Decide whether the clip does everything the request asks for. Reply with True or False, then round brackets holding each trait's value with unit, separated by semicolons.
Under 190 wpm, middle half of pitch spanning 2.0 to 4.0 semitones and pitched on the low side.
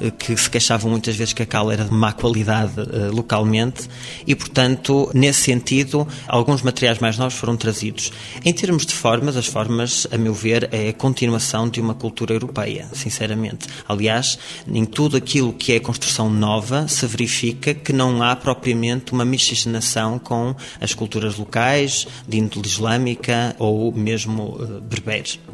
True (155 wpm; 2.6 semitones; 120 Hz)